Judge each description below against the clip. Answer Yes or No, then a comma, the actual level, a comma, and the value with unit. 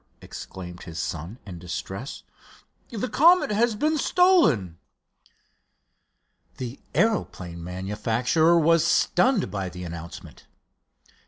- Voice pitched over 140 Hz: No, low, 110 Hz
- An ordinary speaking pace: No, slow, 95 wpm